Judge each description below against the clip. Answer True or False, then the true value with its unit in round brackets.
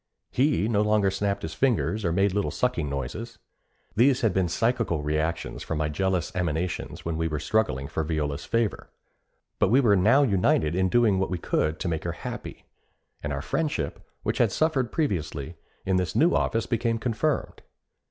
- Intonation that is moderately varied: False (6.1 semitones)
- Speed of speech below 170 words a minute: False (180 wpm)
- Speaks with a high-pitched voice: False (95 Hz)